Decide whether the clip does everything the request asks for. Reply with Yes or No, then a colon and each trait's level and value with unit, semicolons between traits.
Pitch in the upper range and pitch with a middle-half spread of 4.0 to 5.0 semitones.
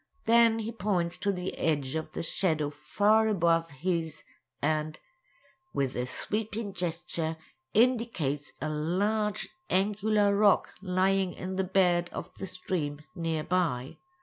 No: medium, 180 Hz; average, 4.4 semitones